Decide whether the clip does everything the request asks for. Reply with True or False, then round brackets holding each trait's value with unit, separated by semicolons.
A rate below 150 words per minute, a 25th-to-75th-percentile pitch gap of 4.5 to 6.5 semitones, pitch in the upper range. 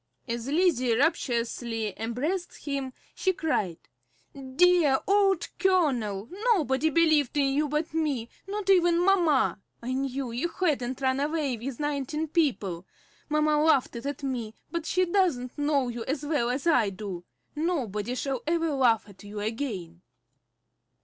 True (140 wpm; 5.2 semitones; 275 Hz)